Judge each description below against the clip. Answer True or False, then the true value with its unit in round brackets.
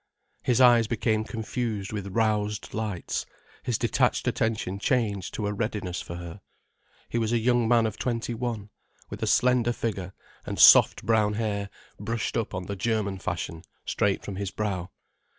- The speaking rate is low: False (165 wpm)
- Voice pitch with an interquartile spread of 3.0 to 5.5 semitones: False (2.5 semitones)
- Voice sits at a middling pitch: False (110 Hz)